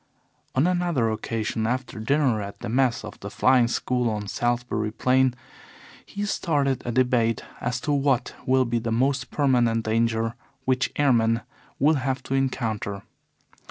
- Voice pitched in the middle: No, low, 125 Hz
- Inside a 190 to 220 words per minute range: No, average, 150 wpm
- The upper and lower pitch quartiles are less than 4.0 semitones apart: Yes, average, 2.7 semitones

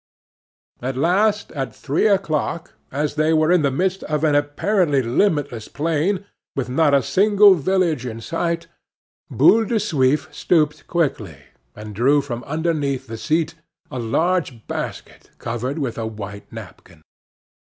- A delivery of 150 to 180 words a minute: No, average, 140 wpm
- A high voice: No, medium, 150 Hz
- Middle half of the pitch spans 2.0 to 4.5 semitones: No, average, 4.9 semitones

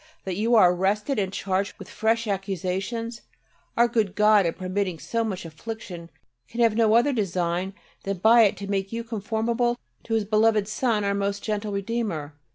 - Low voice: No, high, 210 Hz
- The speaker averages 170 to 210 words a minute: Yes, average, 175 wpm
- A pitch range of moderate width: Yes, average, 3.0 semitones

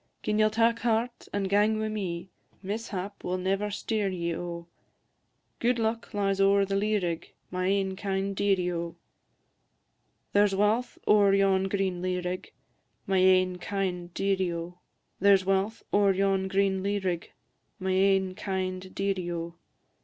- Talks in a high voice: Yes, high, 195 Hz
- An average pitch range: No, narrow, 1.7 semitones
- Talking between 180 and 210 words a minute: No, average, 155 wpm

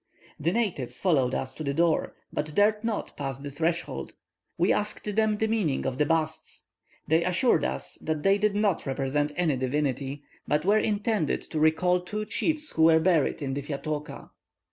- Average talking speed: Yes, average, 180 wpm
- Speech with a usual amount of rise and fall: No, wide, 6.0 semitones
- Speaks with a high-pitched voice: No, medium, 160 Hz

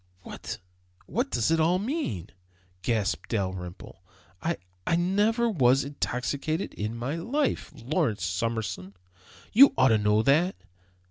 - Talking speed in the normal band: No, slow, 125 wpm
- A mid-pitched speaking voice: No, low, 130 Hz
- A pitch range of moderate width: No, wide, 8.9 semitones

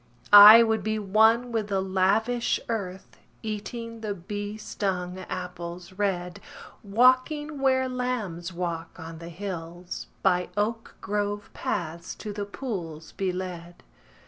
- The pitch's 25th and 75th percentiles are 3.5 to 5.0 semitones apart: Yes, average, 3.8 semitones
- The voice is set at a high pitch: Yes, high, 200 Hz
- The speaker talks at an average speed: No, slow, 125 wpm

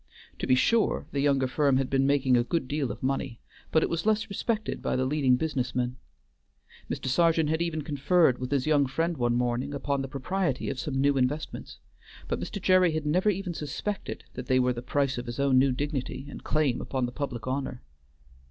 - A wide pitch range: No, average, 3.5 semitones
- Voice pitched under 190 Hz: Yes, medium, 140 Hz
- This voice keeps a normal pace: No, fast, 210 wpm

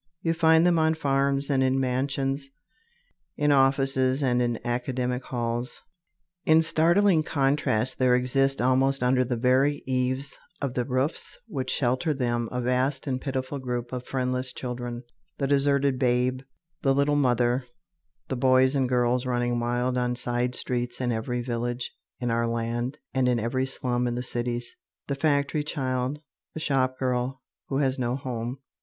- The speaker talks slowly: No, average, 160 wpm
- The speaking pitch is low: Yes, low, 130 Hz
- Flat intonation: Yes, narrow, 1.9 semitones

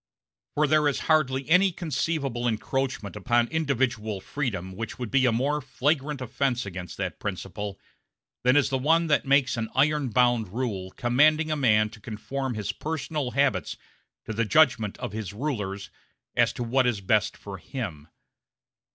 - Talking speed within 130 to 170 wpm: Yes, average, 160 wpm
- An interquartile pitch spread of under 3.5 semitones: No, average, 5.0 semitones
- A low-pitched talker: Yes, low, 125 Hz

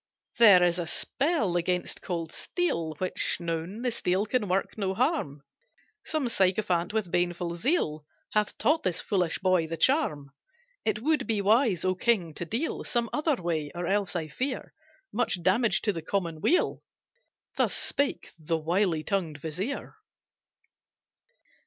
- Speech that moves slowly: No, average, 150 wpm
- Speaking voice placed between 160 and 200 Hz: Yes, medium, 185 Hz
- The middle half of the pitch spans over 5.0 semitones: Yes, wide, 5.4 semitones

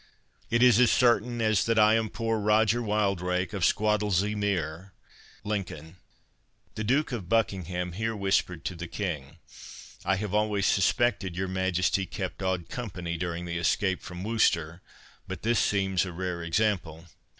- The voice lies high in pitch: No, very low, 95 Hz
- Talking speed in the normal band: Yes, average, 150 wpm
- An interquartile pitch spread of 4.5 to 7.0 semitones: No, average, 3.3 semitones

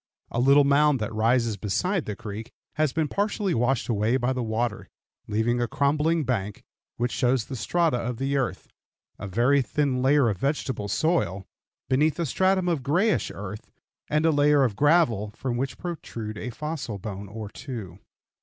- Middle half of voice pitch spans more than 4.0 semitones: Yes, average, 5.1 semitones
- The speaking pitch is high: No, low, 130 Hz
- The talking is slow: No, average, 175 wpm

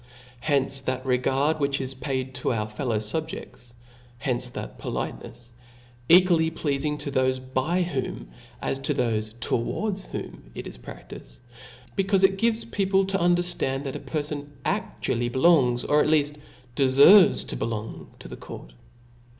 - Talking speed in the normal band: Yes, average, 150 wpm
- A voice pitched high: No, medium, 140 Hz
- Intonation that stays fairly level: No, average, 5.1 semitones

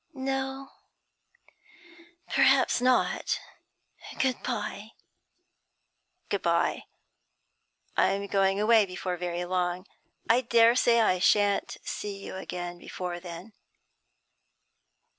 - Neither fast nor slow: No, slow, 90 wpm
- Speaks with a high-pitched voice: Yes, high, 200 Hz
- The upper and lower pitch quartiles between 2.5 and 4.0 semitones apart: No, average, 4.5 semitones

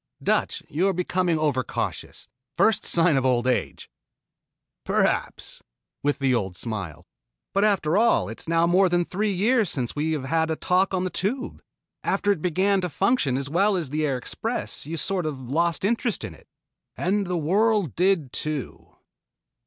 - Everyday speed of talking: Yes, average, 175 wpm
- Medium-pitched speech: Yes, medium, 170 Hz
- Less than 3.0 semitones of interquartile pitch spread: No, wide, 5.4 semitones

